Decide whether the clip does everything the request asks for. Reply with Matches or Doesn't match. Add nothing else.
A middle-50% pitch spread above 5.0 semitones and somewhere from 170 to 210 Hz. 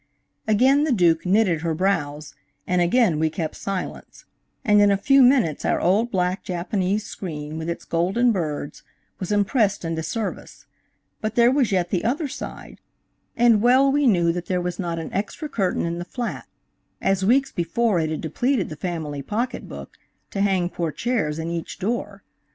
Matches